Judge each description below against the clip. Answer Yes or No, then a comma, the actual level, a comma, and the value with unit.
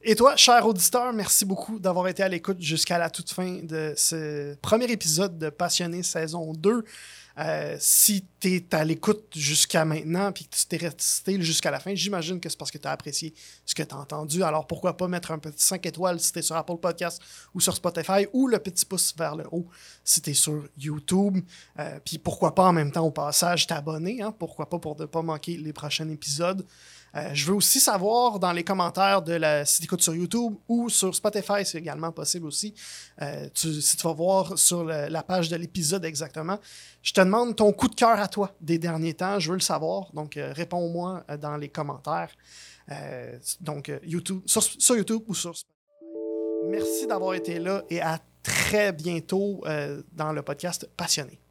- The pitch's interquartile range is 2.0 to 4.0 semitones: Yes, average, 3.5 semitones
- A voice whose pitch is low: No, medium, 175 Hz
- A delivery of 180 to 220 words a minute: Yes, average, 210 wpm